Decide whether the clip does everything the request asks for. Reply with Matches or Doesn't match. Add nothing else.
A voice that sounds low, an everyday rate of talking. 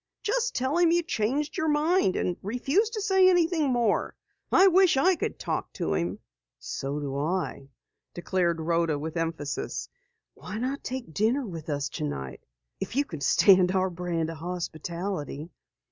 Doesn't match